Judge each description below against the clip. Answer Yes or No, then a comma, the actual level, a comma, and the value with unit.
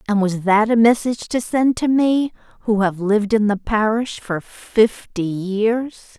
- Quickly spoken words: No, average, 175 wpm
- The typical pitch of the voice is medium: No, high, 220 Hz